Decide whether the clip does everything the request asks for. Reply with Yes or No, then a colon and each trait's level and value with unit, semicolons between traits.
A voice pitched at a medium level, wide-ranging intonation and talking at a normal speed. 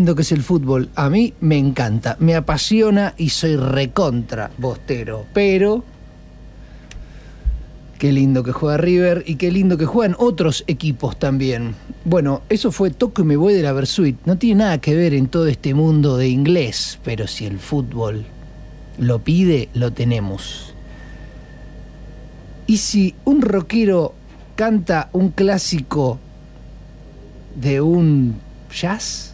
Yes: medium, 150 Hz; wide, 6.0 semitones; average, 135 wpm